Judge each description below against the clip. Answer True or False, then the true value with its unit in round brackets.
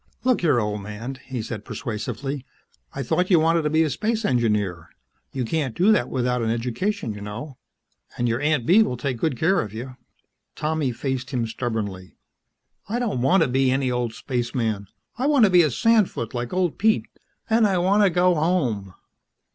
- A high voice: False (130 Hz)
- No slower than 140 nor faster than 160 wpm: False (190 wpm)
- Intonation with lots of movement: True (7.3 semitones)